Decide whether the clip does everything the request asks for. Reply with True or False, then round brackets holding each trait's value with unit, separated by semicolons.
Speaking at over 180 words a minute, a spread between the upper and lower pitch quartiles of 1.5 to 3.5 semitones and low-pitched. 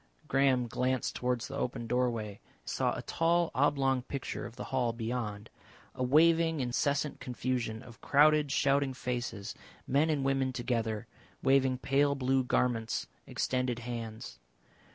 False (135 wpm; 2.5 semitones; 130 Hz)